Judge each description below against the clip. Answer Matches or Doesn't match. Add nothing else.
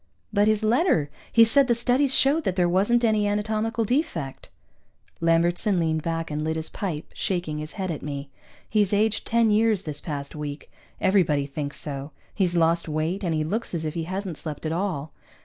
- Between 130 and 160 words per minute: Doesn't match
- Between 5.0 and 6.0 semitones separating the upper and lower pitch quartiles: Matches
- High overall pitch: Doesn't match